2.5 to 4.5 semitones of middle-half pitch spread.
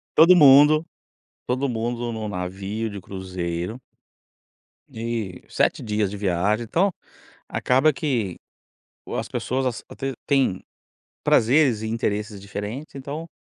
No: average, 5.0 semitones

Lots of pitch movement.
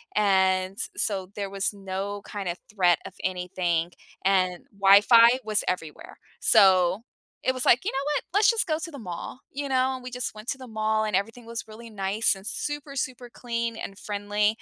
No: average, 4.2 semitones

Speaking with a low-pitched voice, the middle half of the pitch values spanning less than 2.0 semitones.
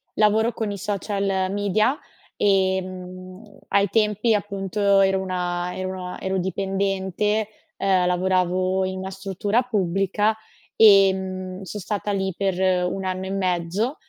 No: high, 190 Hz; narrow, 1.6 semitones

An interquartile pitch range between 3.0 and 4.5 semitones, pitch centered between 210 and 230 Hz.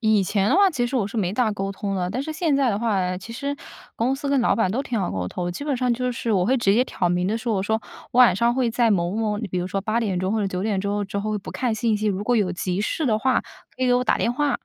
Yes: average, 4.1 semitones; high, 220 Hz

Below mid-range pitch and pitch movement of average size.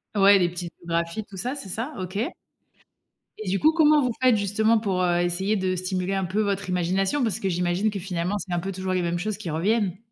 No: high, 195 Hz; average, 3.1 semitones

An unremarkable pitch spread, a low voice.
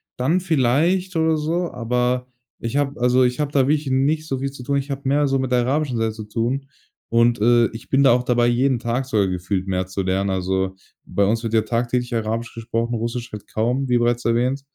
Yes: average, 3.1 semitones; low, 125 Hz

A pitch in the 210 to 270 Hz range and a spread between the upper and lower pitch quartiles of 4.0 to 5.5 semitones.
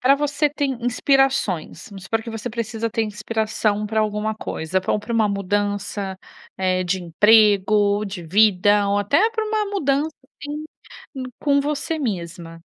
Yes: high, 215 Hz; average, 5.2 semitones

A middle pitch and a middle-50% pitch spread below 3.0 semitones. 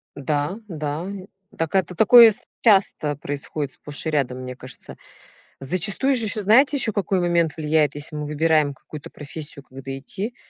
No: medium, 155 Hz; average, 5.3 semitones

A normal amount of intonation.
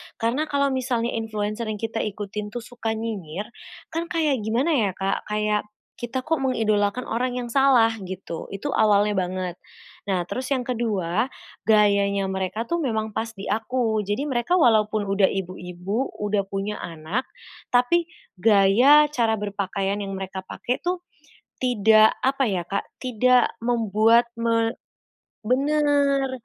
Yes: average, 4.0 semitones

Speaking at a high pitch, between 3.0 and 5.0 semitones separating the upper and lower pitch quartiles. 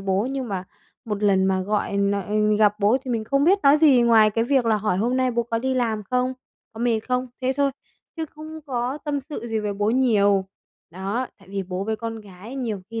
Yes: high, 225 Hz; average, 4.0 semitones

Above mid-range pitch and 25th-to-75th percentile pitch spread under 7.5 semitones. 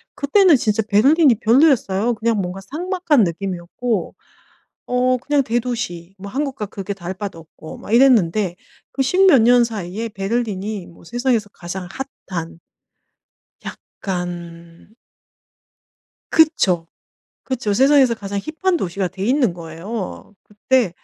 Yes: high, 215 Hz; wide, 5.6 semitones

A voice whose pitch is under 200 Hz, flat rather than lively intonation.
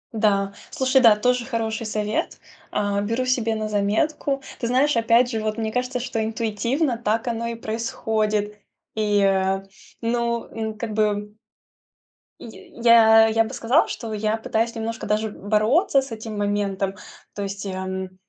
No: high, 220 Hz; narrow, 2.0 semitones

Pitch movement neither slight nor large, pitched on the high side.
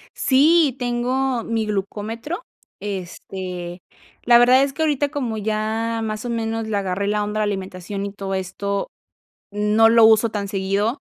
Yes: average, 3.2 semitones; high, 215 Hz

